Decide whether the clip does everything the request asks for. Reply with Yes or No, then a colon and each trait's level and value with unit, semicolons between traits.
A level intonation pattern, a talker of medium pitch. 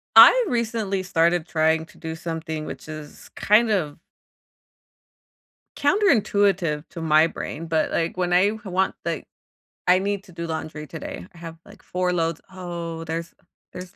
No: average, 3.2 semitones; medium, 170 Hz